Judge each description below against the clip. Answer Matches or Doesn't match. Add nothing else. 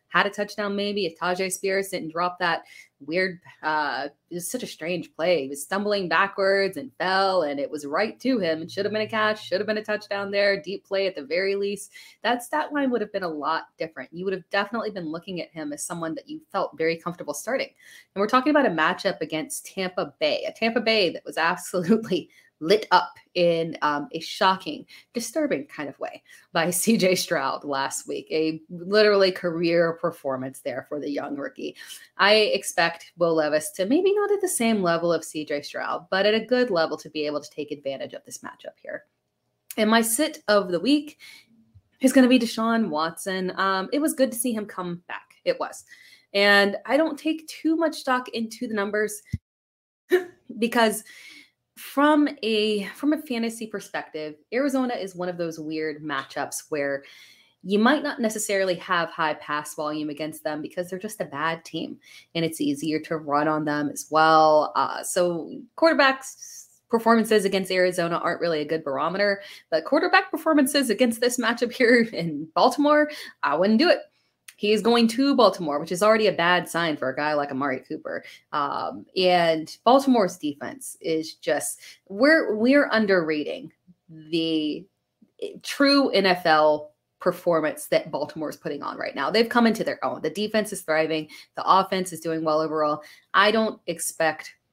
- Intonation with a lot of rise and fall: Matches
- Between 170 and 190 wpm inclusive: Matches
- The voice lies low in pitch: Doesn't match